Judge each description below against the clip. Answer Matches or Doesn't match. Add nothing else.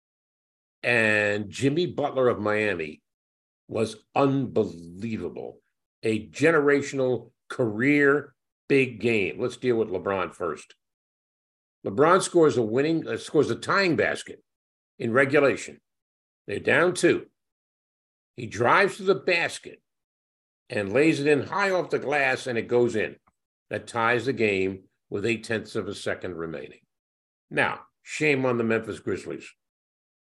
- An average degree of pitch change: Matches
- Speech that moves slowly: Matches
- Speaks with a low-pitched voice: Matches